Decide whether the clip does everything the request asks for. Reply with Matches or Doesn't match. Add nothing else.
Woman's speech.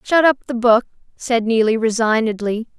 Matches